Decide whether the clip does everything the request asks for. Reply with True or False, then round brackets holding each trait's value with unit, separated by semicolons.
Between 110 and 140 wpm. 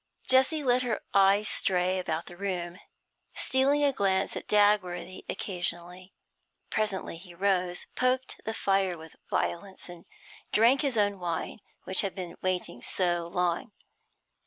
True (135 wpm)